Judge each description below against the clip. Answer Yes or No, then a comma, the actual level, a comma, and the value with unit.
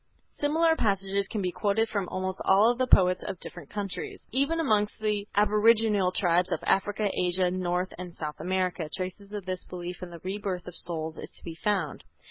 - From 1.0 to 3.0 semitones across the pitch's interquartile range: Yes, average, 2.7 semitones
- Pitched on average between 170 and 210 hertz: Yes, high, 190 Hz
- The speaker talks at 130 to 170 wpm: No, average, 185 wpm